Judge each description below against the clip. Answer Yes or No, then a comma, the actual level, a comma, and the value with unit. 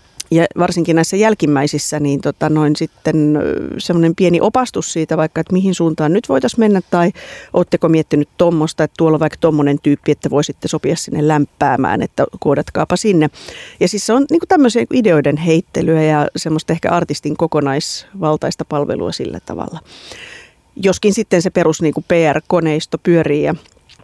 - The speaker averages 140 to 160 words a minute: Yes, average, 150 wpm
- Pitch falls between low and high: Yes, medium, 160 Hz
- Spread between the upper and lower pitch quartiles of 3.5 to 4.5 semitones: No, average, 2.8 semitones